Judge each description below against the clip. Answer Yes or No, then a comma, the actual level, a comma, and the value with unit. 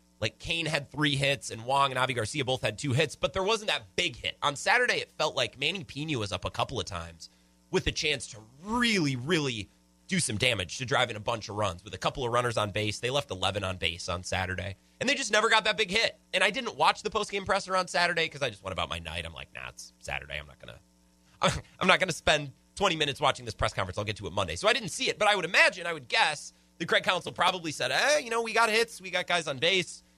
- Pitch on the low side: Yes, low, 125 Hz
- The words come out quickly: Yes, fast, 275 wpm